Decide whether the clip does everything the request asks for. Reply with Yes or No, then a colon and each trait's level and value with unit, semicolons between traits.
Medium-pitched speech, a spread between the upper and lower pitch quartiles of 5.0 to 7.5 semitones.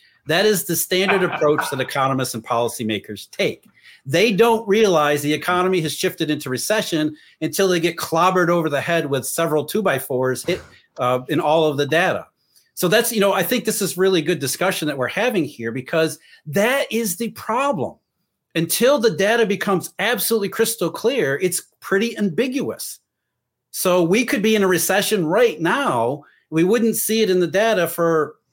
Yes: medium, 180 Hz; wide, 5.5 semitones